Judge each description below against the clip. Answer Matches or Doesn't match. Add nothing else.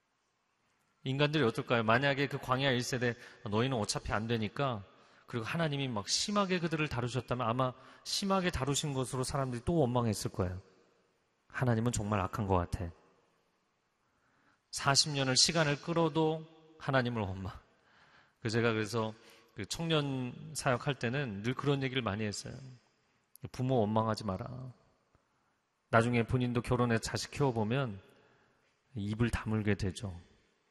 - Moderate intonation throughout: Matches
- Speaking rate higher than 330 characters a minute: Doesn't match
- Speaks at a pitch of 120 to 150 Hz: Matches